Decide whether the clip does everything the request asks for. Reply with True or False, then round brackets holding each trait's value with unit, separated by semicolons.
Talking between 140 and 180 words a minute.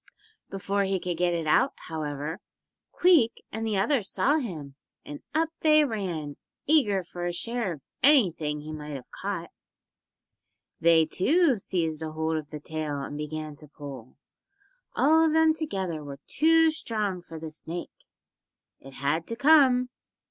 True (155 wpm)